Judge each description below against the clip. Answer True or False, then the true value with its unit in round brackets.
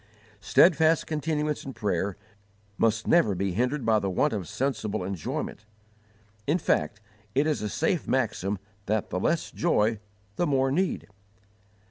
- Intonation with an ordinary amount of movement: False (6.5 semitones)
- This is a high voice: False (115 Hz)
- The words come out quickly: False (140 wpm)